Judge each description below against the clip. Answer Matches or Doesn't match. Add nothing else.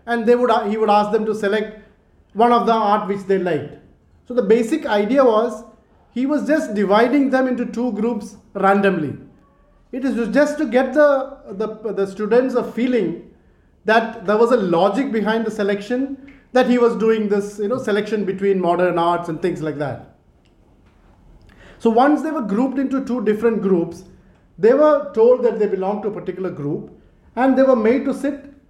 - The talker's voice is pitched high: Matches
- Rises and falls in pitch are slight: Doesn't match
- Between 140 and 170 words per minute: Doesn't match